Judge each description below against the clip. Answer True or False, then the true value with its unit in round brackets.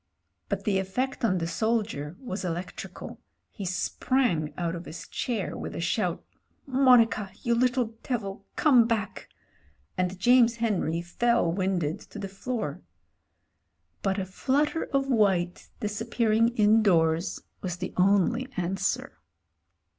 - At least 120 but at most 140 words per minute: True (135 wpm)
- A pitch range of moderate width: True (4.6 semitones)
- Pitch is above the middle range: True (205 Hz)